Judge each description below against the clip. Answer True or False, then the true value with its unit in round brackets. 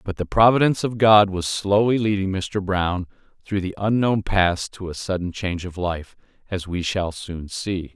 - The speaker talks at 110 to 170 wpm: False (190 wpm)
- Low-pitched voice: True (95 Hz)